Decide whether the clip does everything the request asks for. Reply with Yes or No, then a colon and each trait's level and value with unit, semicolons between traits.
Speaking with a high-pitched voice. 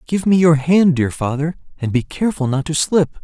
No: medium, 155 Hz